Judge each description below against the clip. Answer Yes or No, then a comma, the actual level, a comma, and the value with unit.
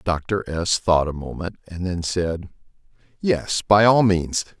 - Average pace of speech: Yes, average, 145 wpm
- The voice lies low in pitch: Yes, very low, 90 Hz